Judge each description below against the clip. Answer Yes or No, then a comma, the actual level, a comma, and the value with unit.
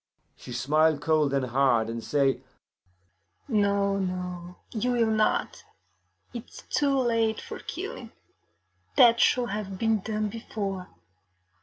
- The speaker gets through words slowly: Yes, slow, 125 wpm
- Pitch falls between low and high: No, high, 195 Hz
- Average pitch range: No, wide, 6.6 semitones